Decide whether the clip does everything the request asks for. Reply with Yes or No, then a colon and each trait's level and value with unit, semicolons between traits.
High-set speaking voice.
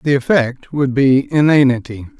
No: low, 135 Hz